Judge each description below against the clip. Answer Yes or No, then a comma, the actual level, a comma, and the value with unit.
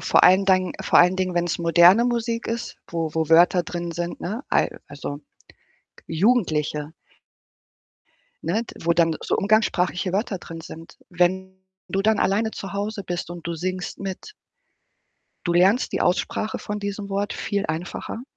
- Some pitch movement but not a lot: Yes, average, 3.0 semitones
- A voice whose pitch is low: No, medium, 185 Hz